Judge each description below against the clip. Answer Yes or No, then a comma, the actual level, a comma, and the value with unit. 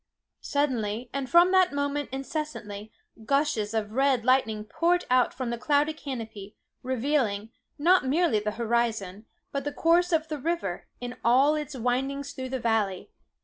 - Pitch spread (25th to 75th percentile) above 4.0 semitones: Yes, average, 4.8 semitones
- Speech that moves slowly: No, average, 150 wpm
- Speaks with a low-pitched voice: No, very high, 260 Hz